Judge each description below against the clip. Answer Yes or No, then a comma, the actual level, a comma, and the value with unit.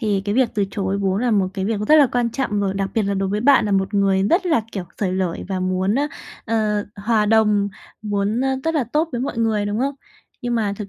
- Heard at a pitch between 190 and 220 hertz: Yes, high, 210 Hz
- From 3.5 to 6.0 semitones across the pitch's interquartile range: No, average, 3.1 semitones